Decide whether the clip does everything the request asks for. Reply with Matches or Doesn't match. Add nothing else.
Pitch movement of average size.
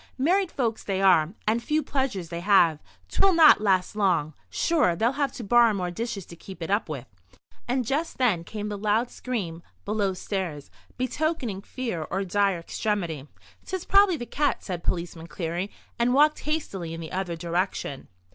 Doesn't match